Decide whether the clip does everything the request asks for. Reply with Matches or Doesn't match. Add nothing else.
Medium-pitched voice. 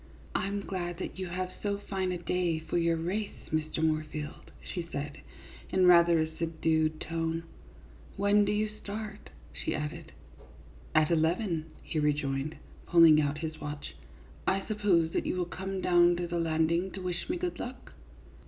Matches